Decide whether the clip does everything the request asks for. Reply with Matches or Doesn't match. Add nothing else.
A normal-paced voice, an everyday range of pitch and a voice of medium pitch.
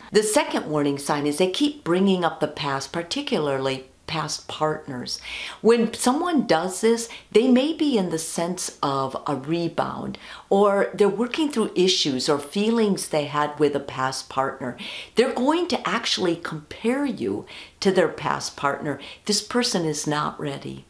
Doesn't match